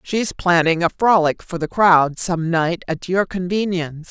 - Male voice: No, female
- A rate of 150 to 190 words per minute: Yes, average, 175 wpm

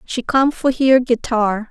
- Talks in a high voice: Yes, high, 245 Hz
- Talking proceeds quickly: No, average, 175 wpm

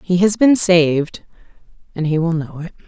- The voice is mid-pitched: Yes, medium, 175 Hz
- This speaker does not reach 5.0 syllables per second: No, 5.2 syllables/s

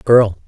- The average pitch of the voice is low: Yes, low, 110 Hz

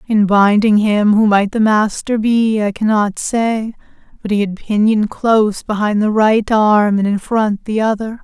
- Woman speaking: Yes, female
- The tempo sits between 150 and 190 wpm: Yes, average, 180 wpm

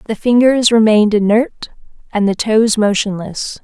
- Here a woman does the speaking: Yes, female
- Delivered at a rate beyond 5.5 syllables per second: No, 4.5 syllables/s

